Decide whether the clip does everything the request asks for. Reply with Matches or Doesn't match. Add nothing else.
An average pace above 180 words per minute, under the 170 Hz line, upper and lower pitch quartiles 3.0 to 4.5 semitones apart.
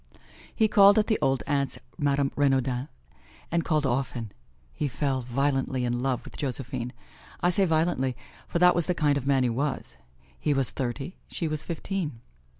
Doesn't match